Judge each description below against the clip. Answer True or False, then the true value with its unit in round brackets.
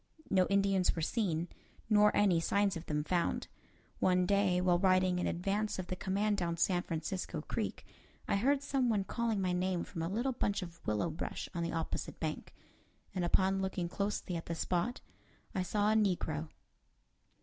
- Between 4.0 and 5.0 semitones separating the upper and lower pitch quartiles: False (2.9 semitones)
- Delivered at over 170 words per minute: True (180 wpm)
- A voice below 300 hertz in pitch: True (185 Hz)